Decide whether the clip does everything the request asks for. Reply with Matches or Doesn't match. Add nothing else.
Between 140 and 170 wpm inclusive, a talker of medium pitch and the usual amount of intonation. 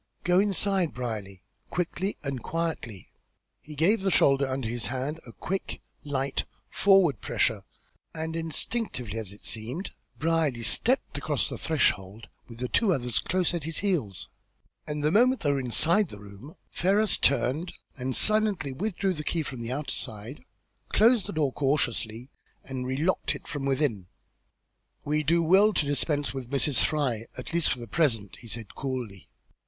Doesn't match